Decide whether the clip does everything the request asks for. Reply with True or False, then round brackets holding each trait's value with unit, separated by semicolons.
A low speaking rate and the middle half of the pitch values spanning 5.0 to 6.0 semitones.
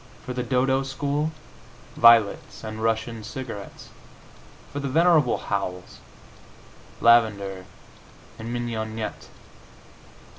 False (85 wpm; 3.3 semitones)